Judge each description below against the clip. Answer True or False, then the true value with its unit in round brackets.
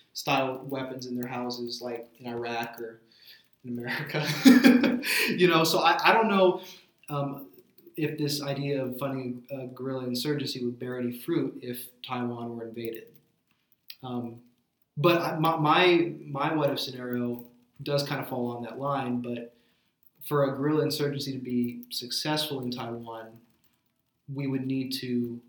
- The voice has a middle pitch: False (130 Hz)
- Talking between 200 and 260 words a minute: False (150 wpm)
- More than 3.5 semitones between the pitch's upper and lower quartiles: False (3.2 semitones)